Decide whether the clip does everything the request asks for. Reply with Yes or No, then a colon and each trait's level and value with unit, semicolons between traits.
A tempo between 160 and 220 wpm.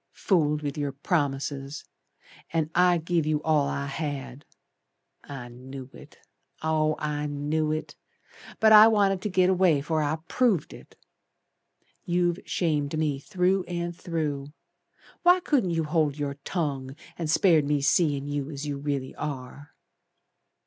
No: average, 140 wpm